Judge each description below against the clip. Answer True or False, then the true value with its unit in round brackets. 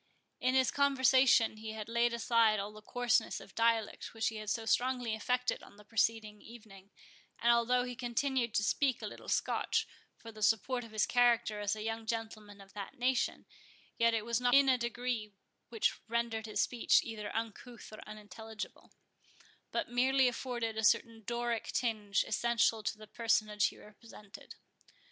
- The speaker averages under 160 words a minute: False (170 wpm)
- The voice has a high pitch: True (230 Hz)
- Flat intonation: True (2.2 semitones)